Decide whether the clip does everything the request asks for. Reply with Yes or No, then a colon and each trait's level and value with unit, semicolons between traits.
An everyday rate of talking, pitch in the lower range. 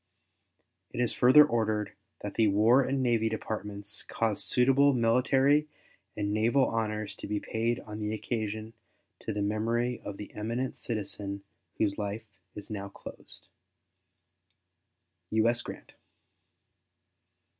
No: slow, 125 wpm; low, 110 Hz